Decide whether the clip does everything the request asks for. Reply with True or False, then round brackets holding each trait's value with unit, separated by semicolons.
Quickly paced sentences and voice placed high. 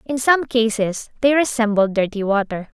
False (150 wpm; 230 Hz)